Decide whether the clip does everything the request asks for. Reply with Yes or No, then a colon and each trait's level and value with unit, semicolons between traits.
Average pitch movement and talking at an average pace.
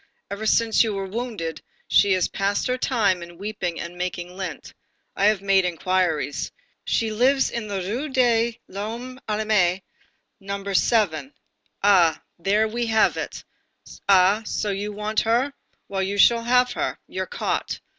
Yes: average, 3.5 semitones; average, 155 wpm